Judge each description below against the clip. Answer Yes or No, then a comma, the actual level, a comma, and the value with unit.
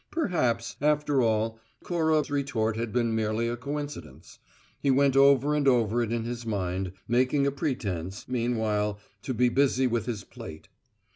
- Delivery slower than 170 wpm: Yes, average, 155 wpm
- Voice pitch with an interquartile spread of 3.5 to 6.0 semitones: Yes, average, 4.0 semitones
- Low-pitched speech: Yes, low, 120 Hz